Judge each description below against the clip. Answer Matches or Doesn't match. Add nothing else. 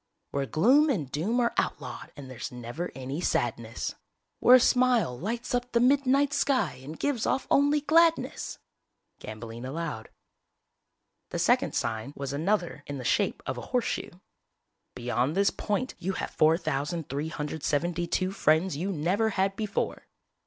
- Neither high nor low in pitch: Matches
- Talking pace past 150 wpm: Doesn't match